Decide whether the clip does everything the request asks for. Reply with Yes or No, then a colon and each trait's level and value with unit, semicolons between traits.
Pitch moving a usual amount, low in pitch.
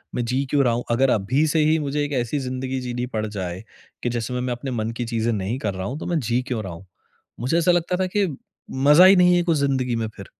Yes: average, 4.2 semitones; low, 125 Hz